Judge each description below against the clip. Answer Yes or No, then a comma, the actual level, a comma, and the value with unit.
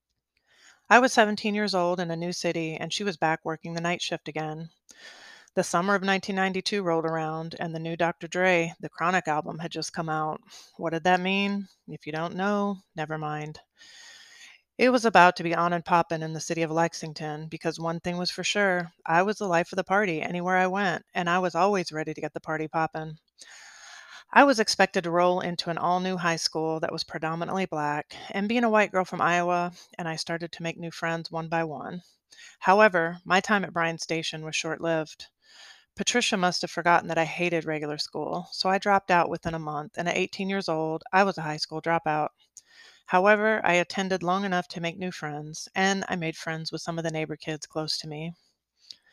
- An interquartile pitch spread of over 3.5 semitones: No, average, 2.8 semitones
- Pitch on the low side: No, medium, 170 Hz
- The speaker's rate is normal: No, fast, 215 wpm